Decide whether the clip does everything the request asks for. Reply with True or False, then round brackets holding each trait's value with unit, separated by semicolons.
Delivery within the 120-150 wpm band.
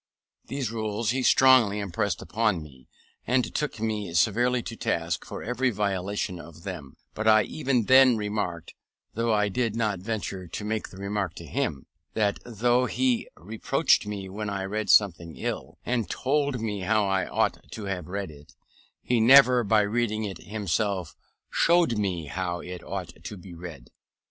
False (170 wpm)